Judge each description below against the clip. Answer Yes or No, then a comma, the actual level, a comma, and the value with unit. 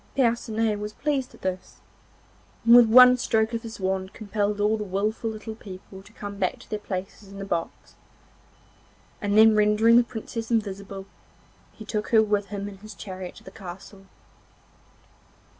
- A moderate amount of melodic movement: No, narrow, 2.2 semitones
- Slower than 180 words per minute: Yes, average, 170 wpm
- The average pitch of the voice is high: Yes, high, 210 Hz